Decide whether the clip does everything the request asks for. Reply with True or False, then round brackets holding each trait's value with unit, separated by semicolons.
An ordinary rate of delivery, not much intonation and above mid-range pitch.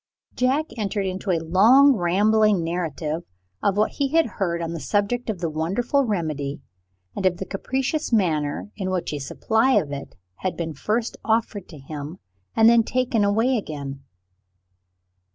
False (160 wpm; 5.6 semitones; 195 Hz)